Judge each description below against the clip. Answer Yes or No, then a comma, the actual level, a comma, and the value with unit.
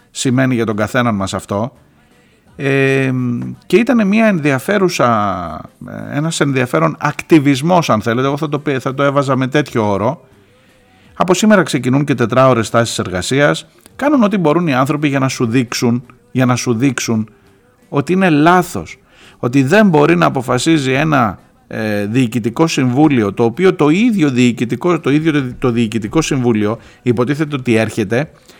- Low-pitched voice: Yes, low, 130 Hz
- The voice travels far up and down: No, average, 4.3 semitones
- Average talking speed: Yes, average, 145 wpm